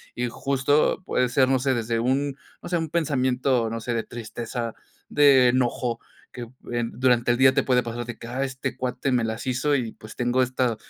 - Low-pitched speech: Yes, low, 125 Hz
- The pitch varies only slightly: Yes, narrow, 2.0 semitones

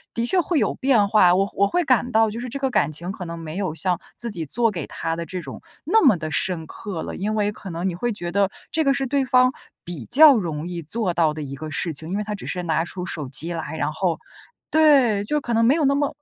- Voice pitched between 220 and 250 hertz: No, high, 195 Hz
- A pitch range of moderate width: No, wide, 6.6 semitones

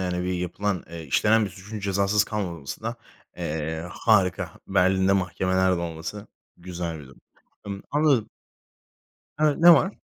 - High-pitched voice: No, very low, 95 Hz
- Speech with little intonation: No, average, 3.5 semitones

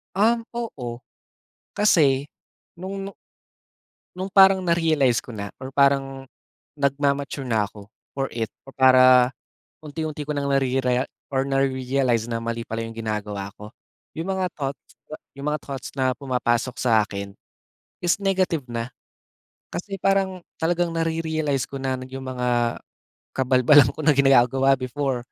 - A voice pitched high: No, low, 135 Hz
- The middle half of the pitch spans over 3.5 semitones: Yes, average, 4.1 semitones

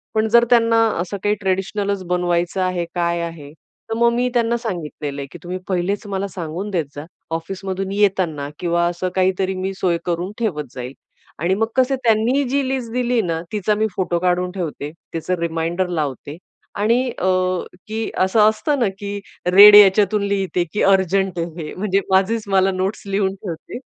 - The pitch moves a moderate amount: Yes, average, 3.4 semitones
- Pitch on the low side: No, high, 190 Hz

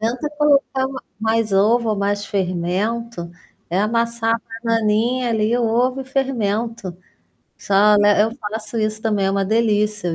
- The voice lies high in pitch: Yes, high, 220 Hz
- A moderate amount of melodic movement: No, narrow, 2.3 semitones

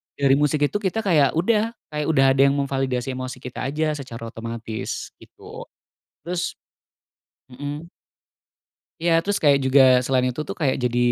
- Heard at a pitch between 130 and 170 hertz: Yes, medium, 140 Hz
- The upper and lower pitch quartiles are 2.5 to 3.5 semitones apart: Yes, average, 3.2 semitones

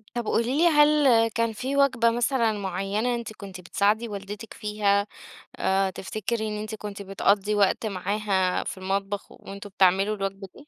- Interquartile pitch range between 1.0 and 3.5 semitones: Yes, average, 2.8 semitones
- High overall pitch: Yes, high, 210 Hz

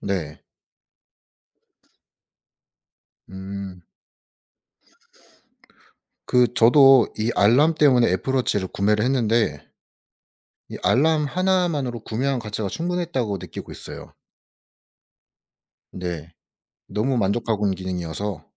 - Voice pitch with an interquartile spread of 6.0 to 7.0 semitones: No, wide, 5.6 semitones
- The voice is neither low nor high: No, low, 115 Hz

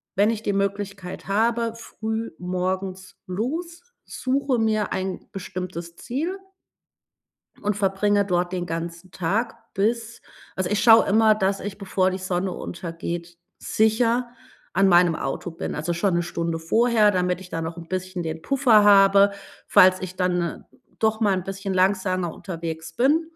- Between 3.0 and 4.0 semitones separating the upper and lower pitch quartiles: Yes, average, 3.5 semitones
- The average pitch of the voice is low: No, high, 195 Hz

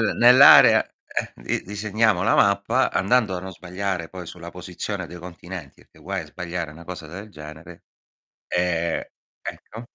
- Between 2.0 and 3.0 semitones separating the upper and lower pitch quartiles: Yes, average, 2.7 semitones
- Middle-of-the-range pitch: No, very low, 90 Hz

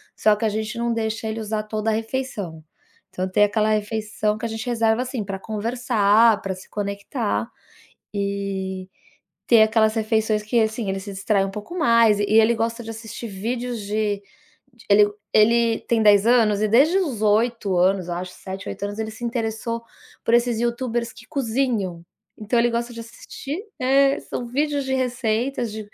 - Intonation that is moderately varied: No, narrow, 2.3 semitones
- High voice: Yes, high, 220 Hz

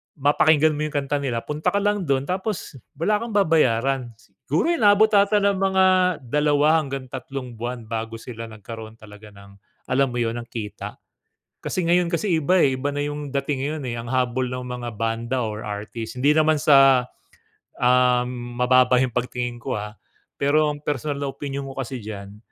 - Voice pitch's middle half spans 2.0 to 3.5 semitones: No, average, 4.3 semitones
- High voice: No, low, 135 Hz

